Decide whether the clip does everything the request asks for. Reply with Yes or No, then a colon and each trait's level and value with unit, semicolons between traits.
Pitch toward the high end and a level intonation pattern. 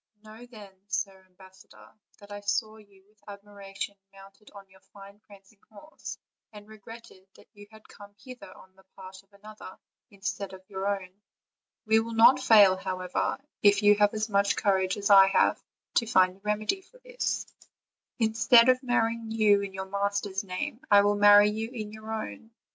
Yes: high, 205 Hz; narrow, 1.9 semitones